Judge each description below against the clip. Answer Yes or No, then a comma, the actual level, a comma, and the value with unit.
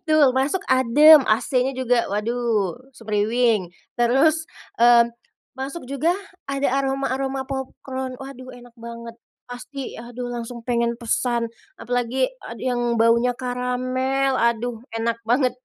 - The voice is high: Yes, high, 245 Hz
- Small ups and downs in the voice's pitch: Yes, narrow, 2.2 semitones